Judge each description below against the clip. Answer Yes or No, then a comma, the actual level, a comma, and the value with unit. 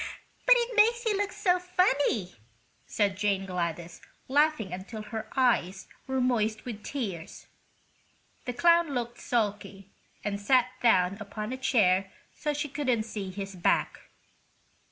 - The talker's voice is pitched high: Yes, high, 225 Hz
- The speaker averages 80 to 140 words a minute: Yes, slow, 135 wpm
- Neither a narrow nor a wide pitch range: No, wide, 6.6 semitones